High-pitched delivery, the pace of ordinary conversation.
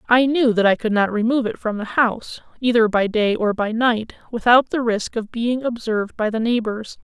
No: high, 225 Hz; fast, 220 wpm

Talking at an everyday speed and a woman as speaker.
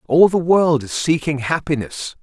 No: average, 160 wpm; male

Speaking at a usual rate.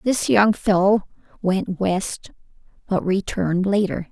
No: slow, 115 wpm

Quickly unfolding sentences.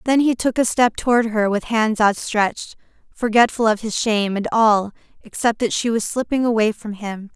No: average, 195 wpm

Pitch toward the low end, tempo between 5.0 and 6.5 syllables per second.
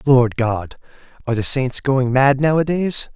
No: low, 130 Hz; 4.4 syllables/s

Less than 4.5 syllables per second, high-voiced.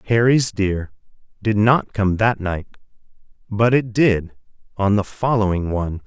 No: 4.3 syllables/s; low, 105 Hz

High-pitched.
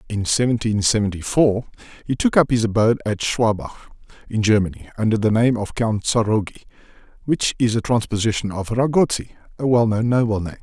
No: low, 110 Hz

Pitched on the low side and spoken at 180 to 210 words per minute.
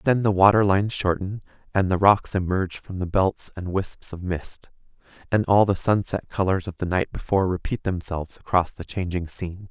Yes: very low, 95 Hz; average, 190 wpm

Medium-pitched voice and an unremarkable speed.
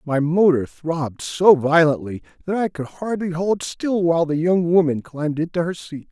Yes: medium, 165 Hz; average, 185 wpm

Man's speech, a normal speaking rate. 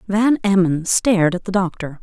No: female; average, 180 wpm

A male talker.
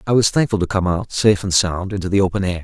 Yes: male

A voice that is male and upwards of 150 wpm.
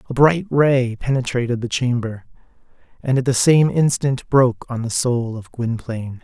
Yes: male; average, 165 wpm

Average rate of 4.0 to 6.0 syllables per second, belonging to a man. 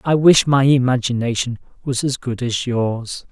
Yes: 4.4 syllables/s; male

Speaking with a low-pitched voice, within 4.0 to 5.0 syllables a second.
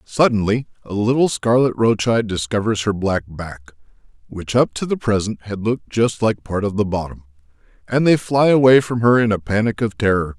No: low, 110 Hz; 5.2 syllables/s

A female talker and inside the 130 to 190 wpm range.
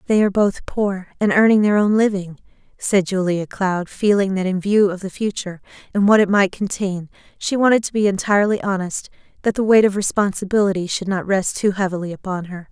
No: female; average, 200 wpm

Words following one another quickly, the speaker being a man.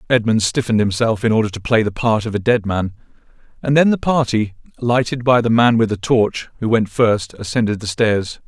Yes: fast, 210 wpm; male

